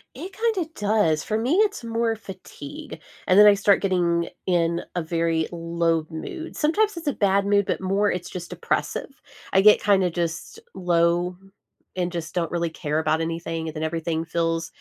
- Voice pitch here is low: No, medium, 180 Hz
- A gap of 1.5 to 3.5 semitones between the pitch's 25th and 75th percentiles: No, average, 4.2 semitones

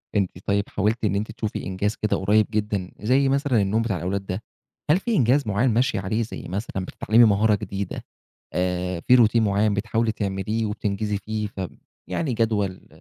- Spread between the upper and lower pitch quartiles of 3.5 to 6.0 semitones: No, narrow, 2.5 semitones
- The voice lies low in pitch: Yes, low, 105 Hz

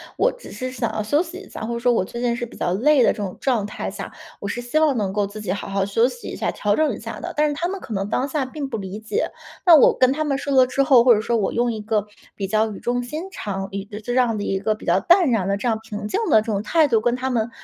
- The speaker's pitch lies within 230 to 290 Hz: Yes, high, 235 Hz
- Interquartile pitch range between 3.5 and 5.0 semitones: Yes, average, 4.3 semitones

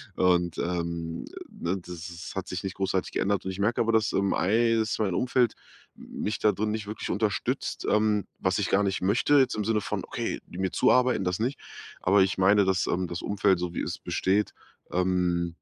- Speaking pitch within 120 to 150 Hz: No, very low, 95 Hz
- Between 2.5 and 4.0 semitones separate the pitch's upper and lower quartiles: Yes, average, 2.9 semitones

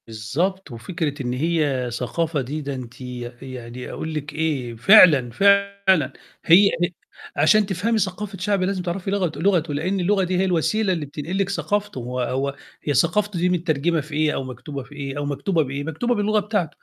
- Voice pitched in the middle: Yes, medium, 160 Hz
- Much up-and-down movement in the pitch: Yes, wide, 5.9 semitones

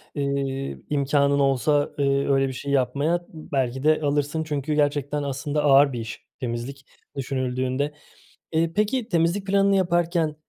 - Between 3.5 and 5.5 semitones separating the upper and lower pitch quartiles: No, narrow, 2.4 semitones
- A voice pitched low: No, medium, 145 Hz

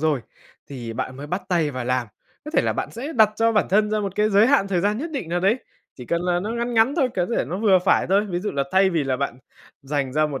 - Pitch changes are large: Yes, wide, 6.6 semitones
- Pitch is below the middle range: No, medium, 185 Hz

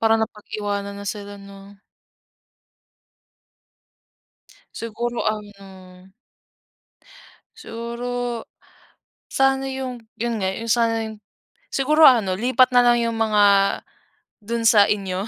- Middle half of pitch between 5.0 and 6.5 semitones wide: No, average, 2.9 semitones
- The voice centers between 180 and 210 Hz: No, high, 225 Hz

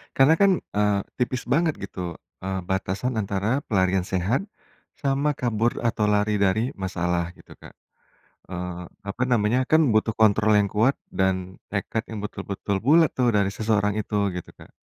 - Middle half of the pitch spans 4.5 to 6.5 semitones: No, average, 4.1 semitones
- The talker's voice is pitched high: No, low, 105 Hz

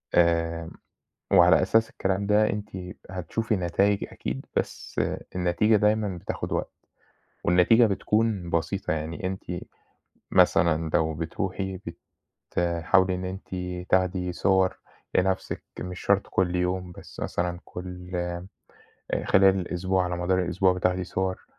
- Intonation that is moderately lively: No, narrow, 1.7 semitones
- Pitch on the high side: No, very low, 90 Hz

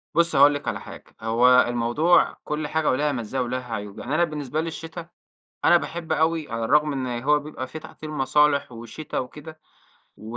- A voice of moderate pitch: Yes, medium, 145 Hz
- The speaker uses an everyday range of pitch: Yes, average, 3.9 semitones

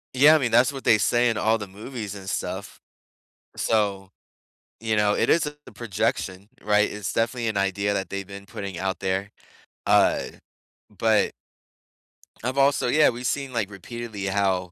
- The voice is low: Yes, low, 105 Hz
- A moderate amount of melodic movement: Yes, average, 3.4 semitones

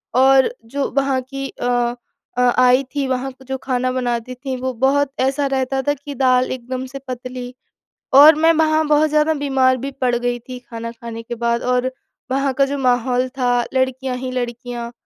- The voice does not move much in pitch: Yes, narrow, 1.7 semitones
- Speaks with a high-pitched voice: Yes, very high, 260 Hz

